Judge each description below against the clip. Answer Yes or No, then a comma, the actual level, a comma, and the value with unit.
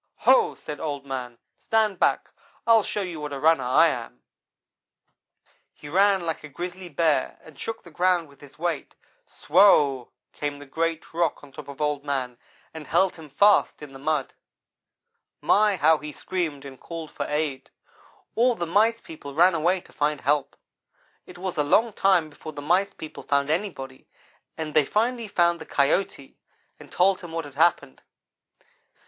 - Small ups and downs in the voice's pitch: No, average, 4.1 semitones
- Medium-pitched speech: Yes, medium, 160 Hz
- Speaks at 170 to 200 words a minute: Yes, average, 175 wpm